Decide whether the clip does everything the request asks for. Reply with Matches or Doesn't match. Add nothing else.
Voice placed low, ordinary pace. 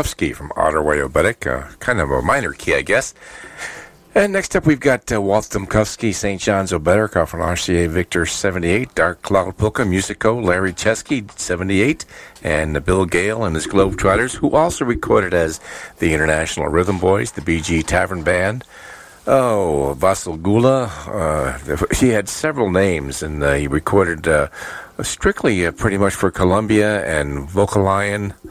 Matches